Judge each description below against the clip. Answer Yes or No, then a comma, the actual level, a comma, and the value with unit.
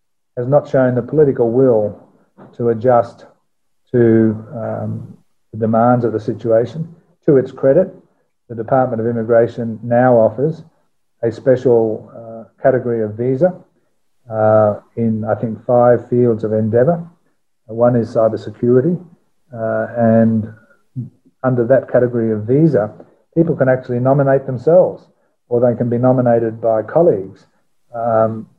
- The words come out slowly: Yes, slow, 130 wpm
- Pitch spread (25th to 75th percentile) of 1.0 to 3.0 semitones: Yes, narrow, 2.6 semitones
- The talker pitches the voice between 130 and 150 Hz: No, low, 120 Hz